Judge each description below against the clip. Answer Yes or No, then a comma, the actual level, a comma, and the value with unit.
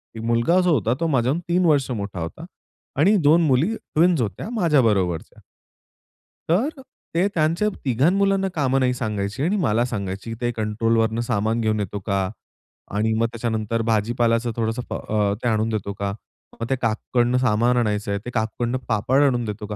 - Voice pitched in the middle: No, low, 115 Hz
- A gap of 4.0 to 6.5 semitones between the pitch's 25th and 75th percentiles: Yes, average, 4.6 semitones